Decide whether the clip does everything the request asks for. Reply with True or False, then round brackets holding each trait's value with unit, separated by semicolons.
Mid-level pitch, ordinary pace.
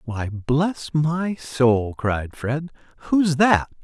False (145 Hz; 125 wpm)